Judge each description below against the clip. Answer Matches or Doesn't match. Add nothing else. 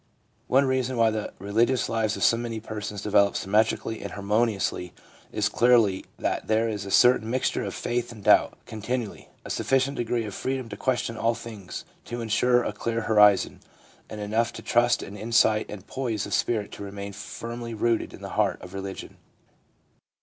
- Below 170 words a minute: Doesn't match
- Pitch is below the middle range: Matches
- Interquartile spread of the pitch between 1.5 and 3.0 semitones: Matches